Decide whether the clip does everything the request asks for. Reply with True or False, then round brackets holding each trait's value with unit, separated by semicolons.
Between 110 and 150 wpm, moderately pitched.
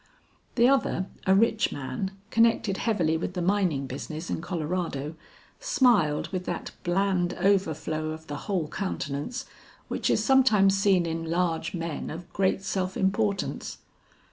True (140 wpm; 180 Hz)